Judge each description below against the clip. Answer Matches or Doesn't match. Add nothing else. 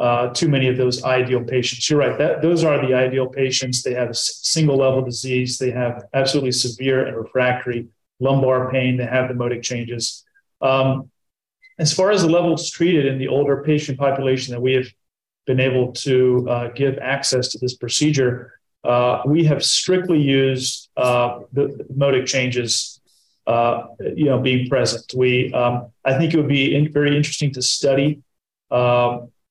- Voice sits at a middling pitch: Doesn't match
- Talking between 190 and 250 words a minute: Doesn't match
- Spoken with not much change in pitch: Matches